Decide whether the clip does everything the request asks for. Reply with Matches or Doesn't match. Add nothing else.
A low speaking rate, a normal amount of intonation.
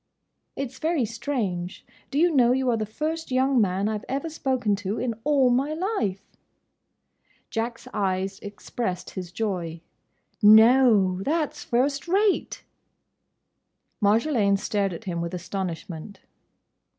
Doesn't match